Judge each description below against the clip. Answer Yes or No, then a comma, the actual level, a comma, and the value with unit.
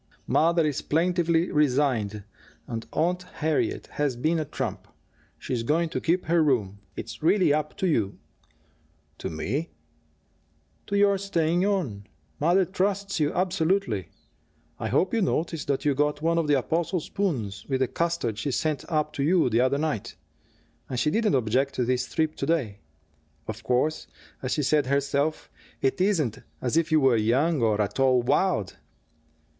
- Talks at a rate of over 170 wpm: No, average, 165 wpm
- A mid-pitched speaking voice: Yes, medium, 150 Hz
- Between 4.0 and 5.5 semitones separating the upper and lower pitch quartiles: Yes, average, 5.1 semitones